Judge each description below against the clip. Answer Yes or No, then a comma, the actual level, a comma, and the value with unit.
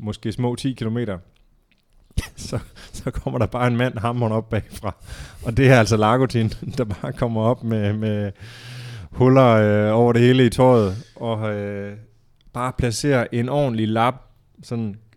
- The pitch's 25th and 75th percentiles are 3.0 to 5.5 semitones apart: No, narrow, 2.4 semitones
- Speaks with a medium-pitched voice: No, low, 115 Hz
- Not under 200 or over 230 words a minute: No, average, 160 wpm